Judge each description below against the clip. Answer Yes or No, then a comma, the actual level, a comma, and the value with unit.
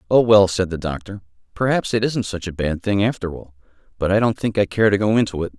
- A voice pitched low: Yes, very low, 95 Hz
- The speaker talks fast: Yes, fast, 260 wpm